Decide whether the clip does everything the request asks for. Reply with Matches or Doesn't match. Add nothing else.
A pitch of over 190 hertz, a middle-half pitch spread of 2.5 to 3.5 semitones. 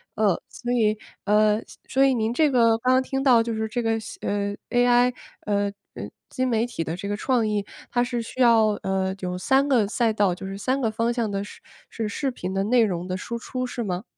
Matches